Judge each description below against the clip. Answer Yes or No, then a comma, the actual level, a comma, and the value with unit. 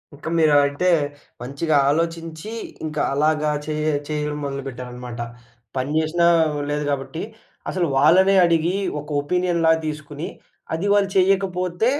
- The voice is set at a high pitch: No, medium, 155 Hz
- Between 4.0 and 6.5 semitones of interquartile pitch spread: No, average, 3.2 semitones